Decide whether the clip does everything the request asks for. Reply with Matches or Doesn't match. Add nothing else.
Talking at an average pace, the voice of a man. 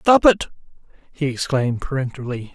Doesn't match